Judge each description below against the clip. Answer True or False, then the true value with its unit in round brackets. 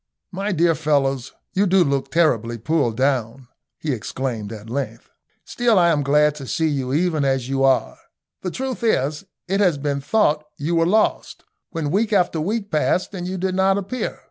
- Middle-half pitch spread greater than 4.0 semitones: True (5.6 semitones)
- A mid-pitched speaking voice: True (155 Hz)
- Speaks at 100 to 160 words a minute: False (190 wpm)